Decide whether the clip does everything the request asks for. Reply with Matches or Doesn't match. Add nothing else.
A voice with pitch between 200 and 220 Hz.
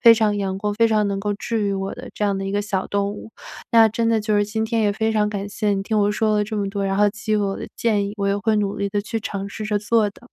Matches